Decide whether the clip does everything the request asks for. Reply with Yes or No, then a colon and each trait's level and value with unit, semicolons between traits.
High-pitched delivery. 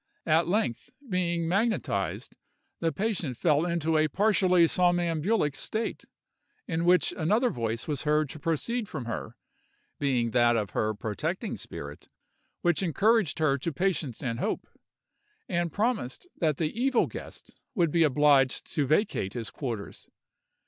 No: medium, 160 Hz